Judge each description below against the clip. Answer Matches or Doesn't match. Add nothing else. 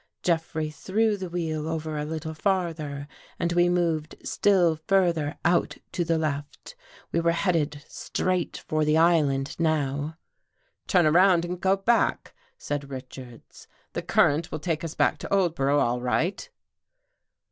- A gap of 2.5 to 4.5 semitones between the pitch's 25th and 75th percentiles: Matches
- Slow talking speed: Doesn't match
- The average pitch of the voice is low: Doesn't match